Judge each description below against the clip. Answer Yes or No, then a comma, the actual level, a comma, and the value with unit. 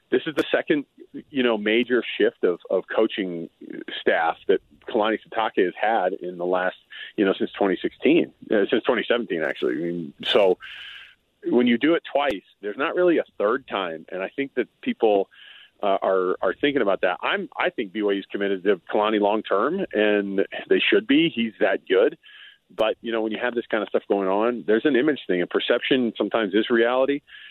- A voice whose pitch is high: No, low, 120 Hz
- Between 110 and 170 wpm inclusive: No, average, 200 wpm